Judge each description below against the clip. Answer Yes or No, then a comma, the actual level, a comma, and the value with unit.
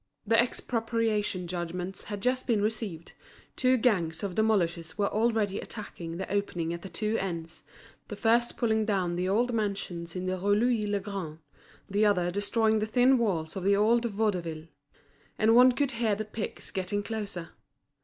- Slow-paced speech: No, average, 170 wpm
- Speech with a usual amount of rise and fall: Yes, average, 3.7 semitones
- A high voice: Yes, high, 205 Hz